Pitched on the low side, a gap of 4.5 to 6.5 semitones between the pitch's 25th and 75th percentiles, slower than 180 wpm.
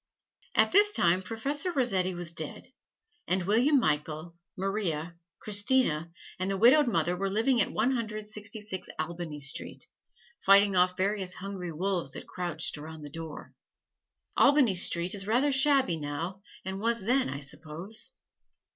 No: high, 190 Hz; average, 4.9 semitones; average, 145 wpm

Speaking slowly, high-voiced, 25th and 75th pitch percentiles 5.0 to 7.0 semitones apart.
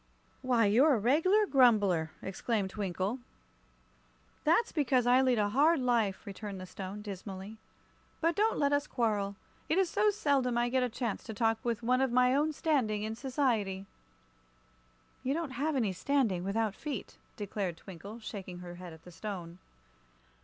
No: average, 165 wpm; high, 230 Hz; average, 5.3 semitones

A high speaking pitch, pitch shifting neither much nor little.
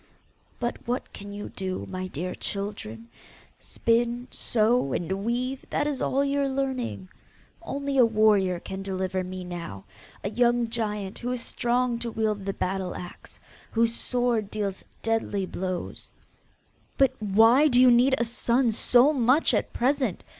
Yes: high, 225 Hz; average, 4.4 semitones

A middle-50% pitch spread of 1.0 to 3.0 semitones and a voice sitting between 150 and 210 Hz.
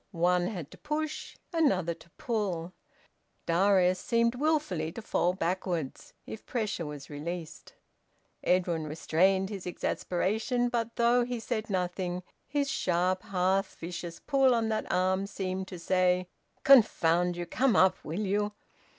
No: average, 4.4 semitones; medium, 185 Hz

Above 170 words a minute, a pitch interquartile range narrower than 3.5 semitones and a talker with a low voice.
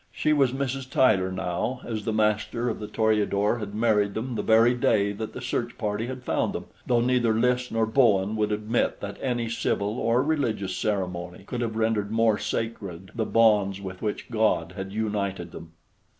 Yes: average, 185 wpm; average, 2.8 semitones; low, 110 Hz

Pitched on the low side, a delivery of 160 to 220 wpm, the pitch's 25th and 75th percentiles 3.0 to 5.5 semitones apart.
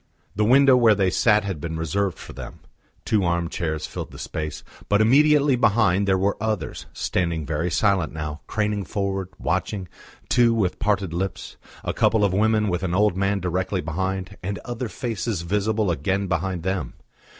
Yes: low, 100 Hz; average, 170 wpm; average, 3.3 semitones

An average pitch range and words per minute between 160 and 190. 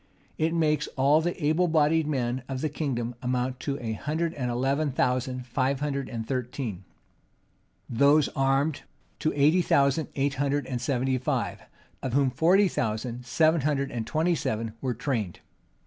Yes: average, 3.4 semitones; average, 165 wpm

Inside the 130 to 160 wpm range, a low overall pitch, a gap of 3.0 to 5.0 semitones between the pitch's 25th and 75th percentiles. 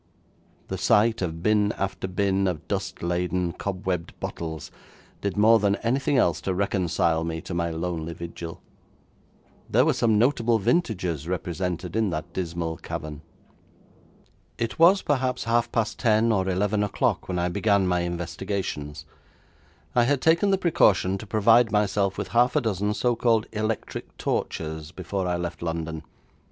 Yes: average, 150 wpm; very low, 95 Hz; average, 4.5 semitones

